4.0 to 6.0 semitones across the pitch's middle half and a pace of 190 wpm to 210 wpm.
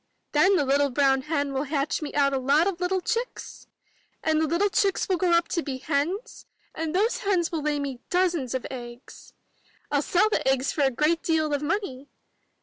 Yes: average, 4.4 semitones; fast, 205 wpm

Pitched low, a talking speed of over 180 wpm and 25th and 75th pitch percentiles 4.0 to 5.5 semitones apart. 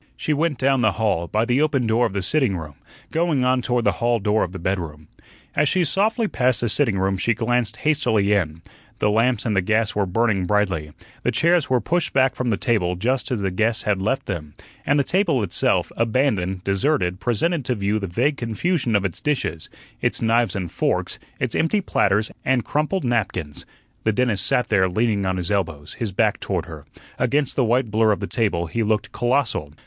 Yes: low, 110 Hz; fast, 205 wpm; average, 5.1 semitones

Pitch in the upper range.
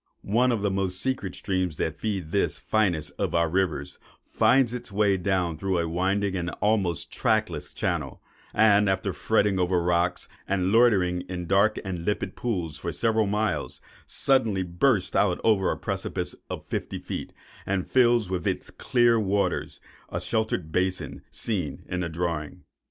No: very low, 95 Hz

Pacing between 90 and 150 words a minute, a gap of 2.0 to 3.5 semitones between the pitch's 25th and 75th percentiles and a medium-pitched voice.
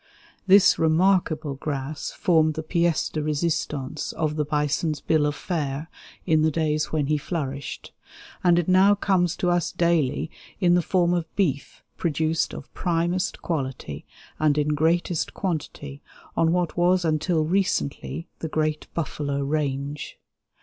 Yes: average, 145 wpm; average, 2.8 semitones; medium, 155 Hz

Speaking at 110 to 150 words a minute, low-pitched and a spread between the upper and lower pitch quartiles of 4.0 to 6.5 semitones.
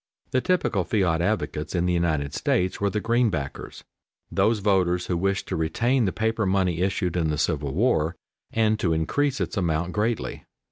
No: average, 175 wpm; very low, 95 Hz; average, 4.9 semitones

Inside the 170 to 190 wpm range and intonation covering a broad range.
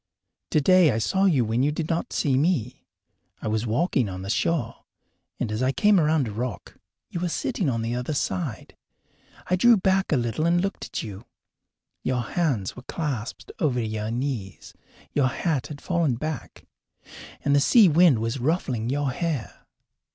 Yes: average, 175 wpm; wide, 6.3 semitones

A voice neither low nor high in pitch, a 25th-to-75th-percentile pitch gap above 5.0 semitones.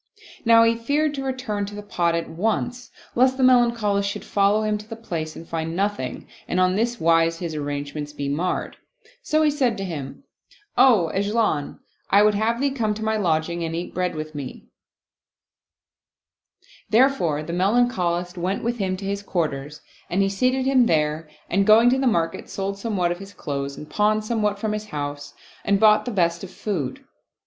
No: high, 200 Hz; wide, 5.5 semitones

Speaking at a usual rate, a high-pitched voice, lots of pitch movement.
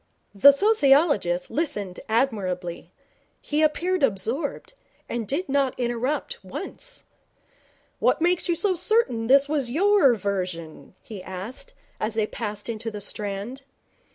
No: slow, 125 wpm; high, 245 Hz; wide, 7.0 semitones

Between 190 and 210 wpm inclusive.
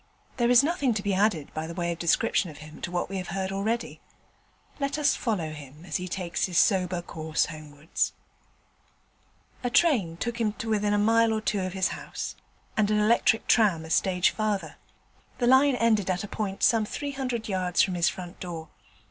Yes: average, 200 wpm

